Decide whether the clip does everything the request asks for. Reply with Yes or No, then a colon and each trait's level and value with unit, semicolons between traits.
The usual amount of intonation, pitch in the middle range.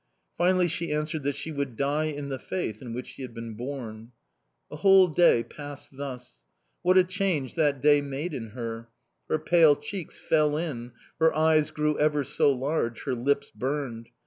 Yes: average, 3.8 semitones; medium, 145 Hz